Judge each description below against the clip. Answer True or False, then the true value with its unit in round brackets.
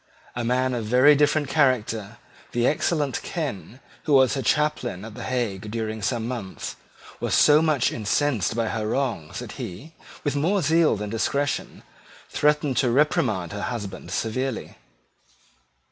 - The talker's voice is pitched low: True (125 Hz)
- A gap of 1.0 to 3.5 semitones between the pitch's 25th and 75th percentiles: False (4.9 semitones)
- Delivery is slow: False (150 wpm)